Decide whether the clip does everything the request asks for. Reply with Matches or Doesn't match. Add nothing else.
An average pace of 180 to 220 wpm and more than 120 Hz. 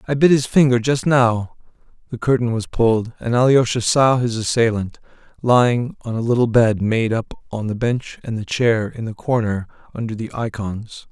Doesn't match